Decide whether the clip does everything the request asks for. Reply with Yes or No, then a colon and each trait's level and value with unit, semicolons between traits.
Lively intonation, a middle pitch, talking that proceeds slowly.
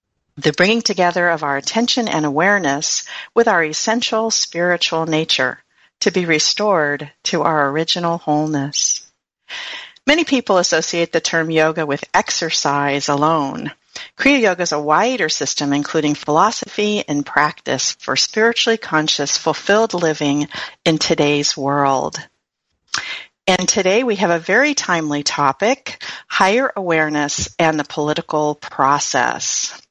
No: average, 5.0 semitones; medium, 160 Hz; slow, 120 wpm